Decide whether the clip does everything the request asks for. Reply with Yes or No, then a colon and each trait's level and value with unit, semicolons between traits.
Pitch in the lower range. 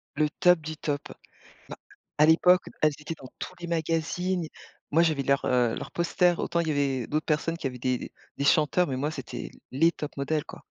No: medium, 155 Hz